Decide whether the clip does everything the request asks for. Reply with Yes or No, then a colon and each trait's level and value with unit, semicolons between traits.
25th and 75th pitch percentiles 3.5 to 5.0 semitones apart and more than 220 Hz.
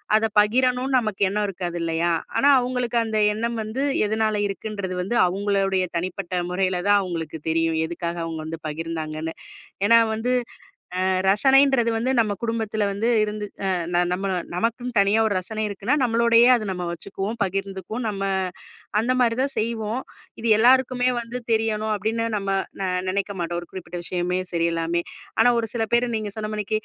No: average, 4.1 semitones; high, 210 Hz